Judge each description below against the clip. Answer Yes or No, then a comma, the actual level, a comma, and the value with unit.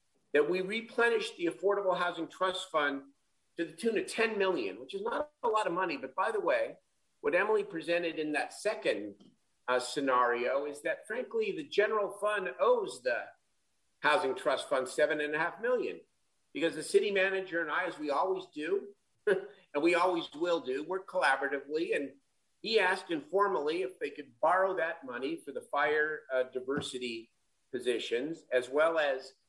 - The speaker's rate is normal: Yes, average, 175 wpm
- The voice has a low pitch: No, medium, 185 Hz